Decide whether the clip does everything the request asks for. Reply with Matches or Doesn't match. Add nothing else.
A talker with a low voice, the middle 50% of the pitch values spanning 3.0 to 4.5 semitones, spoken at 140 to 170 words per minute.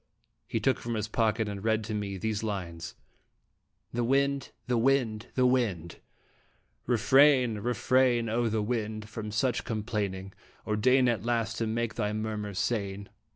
Doesn't match